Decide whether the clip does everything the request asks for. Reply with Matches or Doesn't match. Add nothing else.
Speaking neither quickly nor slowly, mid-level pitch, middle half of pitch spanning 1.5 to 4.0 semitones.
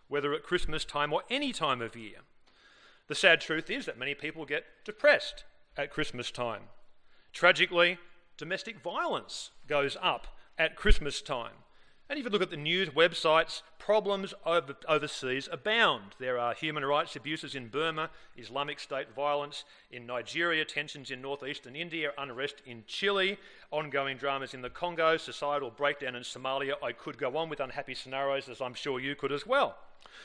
Matches